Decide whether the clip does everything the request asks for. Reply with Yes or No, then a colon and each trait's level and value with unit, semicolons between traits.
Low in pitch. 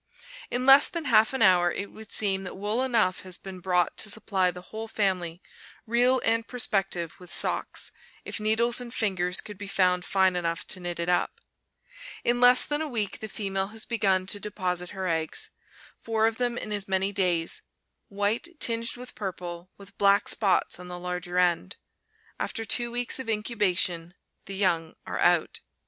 No: high, 200 Hz